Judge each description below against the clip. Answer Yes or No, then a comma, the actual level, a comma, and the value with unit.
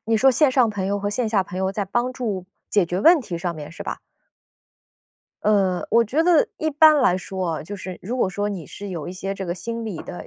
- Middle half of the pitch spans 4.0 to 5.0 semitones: Yes, average, 4.3 semitones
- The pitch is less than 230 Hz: Yes, high, 200 Hz